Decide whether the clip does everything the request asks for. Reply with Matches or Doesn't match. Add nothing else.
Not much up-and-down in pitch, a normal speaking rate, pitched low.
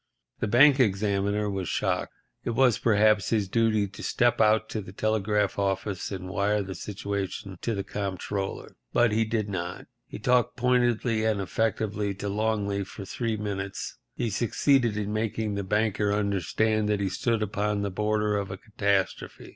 Matches